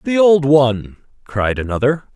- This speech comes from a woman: No, male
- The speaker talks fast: No, average, 140 wpm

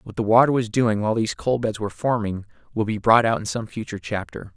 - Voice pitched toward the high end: No, low, 110 Hz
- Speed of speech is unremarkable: No, fast, 250 wpm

